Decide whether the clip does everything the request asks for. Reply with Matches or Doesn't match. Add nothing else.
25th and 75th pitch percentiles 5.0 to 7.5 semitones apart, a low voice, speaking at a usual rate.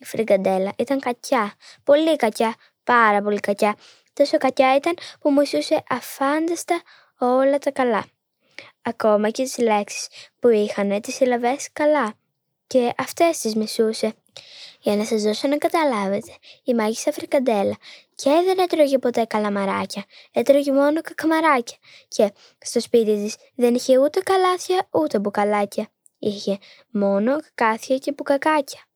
Doesn't match